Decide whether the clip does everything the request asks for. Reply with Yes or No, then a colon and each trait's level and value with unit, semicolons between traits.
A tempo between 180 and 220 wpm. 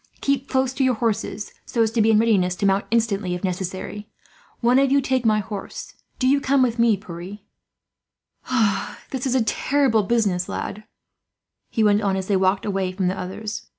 Yes: average, 190 wpm